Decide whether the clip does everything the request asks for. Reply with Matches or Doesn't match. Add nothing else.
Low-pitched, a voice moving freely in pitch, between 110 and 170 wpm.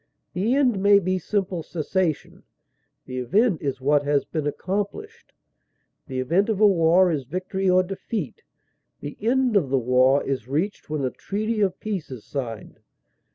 Doesn't match